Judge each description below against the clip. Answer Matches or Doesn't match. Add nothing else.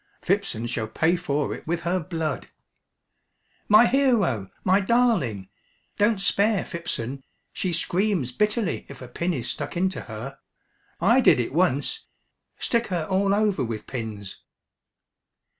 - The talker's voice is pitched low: Doesn't match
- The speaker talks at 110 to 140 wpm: Matches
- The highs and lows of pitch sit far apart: Matches